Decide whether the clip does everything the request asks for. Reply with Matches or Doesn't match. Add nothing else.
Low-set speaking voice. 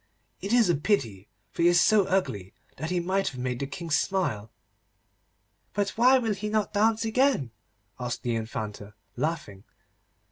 Doesn't match